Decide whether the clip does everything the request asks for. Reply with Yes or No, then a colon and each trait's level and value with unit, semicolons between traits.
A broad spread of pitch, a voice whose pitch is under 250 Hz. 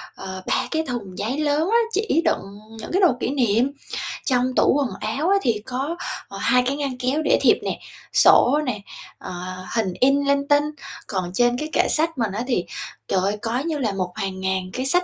No: wide, 5.8 semitones; very high, 255 Hz